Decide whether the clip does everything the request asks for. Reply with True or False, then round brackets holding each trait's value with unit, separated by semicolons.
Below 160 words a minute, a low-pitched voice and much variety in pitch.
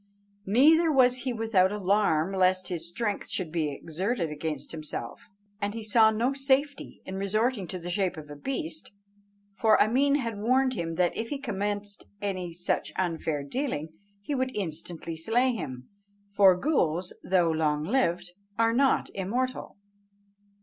False (150 wpm; 200 Hz; 6.3 semitones)